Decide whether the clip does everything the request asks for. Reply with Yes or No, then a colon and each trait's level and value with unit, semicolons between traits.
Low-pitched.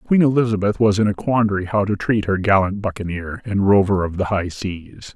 Yes: low, 100 Hz